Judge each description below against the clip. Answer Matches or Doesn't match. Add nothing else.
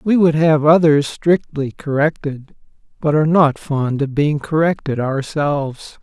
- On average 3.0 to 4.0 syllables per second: Doesn't match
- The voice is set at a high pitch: Doesn't match